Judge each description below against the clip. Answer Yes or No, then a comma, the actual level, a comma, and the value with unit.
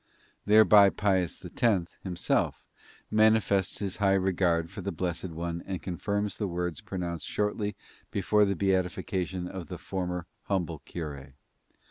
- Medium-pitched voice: No, very low, 95 Hz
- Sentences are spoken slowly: Yes, slow, 130 wpm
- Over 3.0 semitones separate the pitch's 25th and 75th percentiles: No, average, 2.7 semitones